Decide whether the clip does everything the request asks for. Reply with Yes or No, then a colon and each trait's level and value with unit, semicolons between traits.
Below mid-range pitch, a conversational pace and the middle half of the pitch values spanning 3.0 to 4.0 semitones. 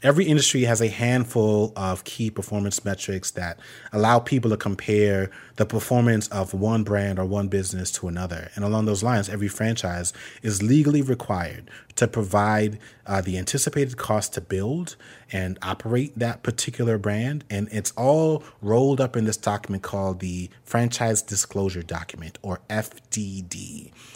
Yes: low, 105 Hz; average, 150 wpm; average, 3.5 semitones